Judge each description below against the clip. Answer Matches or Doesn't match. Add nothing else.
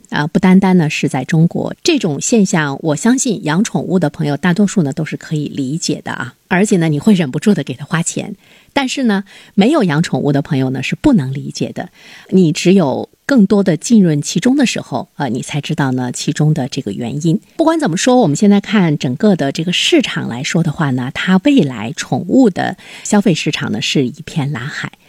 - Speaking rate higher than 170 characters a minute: Matches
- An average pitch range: Doesn't match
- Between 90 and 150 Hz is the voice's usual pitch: Doesn't match